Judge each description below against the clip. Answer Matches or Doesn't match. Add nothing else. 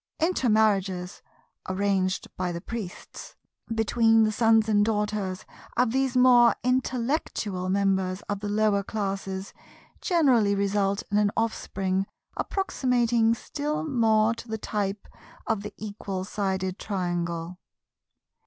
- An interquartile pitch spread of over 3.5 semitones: Doesn't match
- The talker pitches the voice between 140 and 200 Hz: Doesn't match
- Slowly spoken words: Matches